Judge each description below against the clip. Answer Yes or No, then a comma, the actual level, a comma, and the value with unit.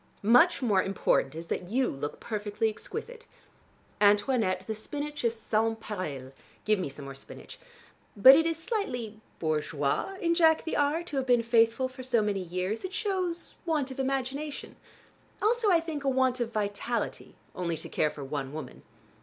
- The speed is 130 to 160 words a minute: No, average, 170 wpm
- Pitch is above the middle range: Yes, high, 230 Hz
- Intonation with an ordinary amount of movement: No, wide, 7.3 semitones